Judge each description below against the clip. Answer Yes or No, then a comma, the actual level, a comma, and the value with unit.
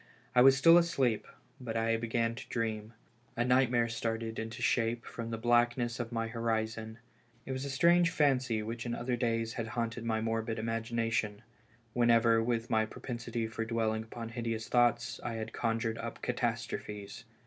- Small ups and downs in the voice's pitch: Yes, narrow, 1.2 semitones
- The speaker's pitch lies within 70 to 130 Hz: Yes, low, 115 Hz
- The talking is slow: No, average, 165 wpm